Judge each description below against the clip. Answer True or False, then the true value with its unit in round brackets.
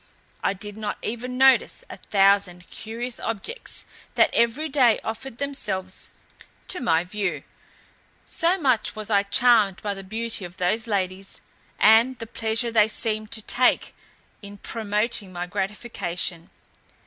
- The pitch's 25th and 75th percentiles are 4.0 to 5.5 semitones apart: False (3.2 semitones)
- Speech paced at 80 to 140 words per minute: True (135 wpm)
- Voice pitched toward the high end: True (215 Hz)